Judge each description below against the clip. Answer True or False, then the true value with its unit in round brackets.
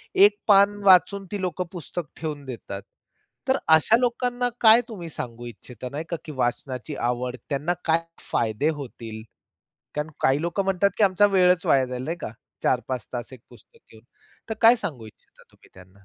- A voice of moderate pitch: True (155 Hz)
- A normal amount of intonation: False (8.0 semitones)